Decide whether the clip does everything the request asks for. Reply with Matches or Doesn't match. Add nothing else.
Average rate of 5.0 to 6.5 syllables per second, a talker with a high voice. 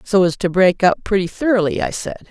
Matches